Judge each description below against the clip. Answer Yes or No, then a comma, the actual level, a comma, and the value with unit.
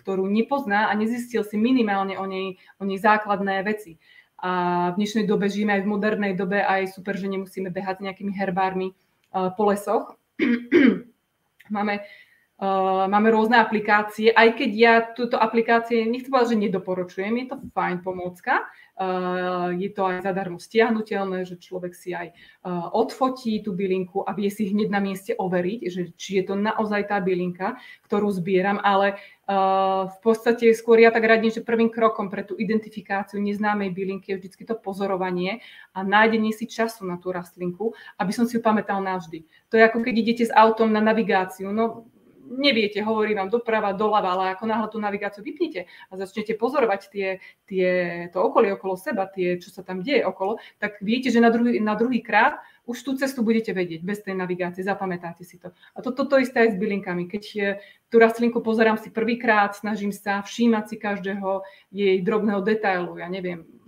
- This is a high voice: Yes, high, 205 Hz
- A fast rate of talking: Yes, fast, 180 wpm